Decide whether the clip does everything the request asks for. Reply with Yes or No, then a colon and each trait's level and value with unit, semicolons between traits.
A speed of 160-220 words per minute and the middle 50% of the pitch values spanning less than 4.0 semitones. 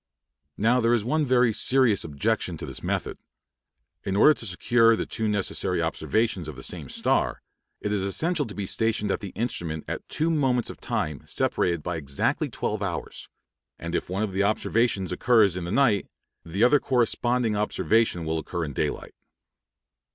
No: average, 175 wpm; average, 5.1 semitones